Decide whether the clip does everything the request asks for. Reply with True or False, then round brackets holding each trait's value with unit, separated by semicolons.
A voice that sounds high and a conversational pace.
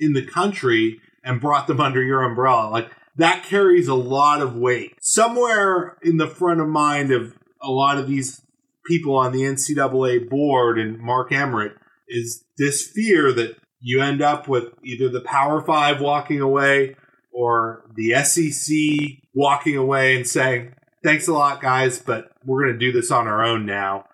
False (135 Hz; 175 wpm)